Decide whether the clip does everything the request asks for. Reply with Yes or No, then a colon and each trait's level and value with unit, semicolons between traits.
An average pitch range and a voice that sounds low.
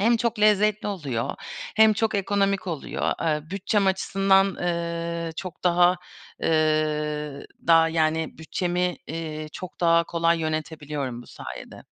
No: average, 3.7 semitones; medium, 170 Hz